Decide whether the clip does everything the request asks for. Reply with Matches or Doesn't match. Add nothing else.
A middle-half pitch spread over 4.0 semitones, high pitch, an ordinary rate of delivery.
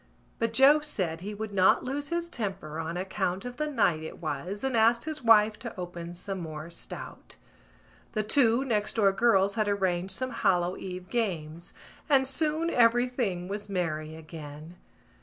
Matches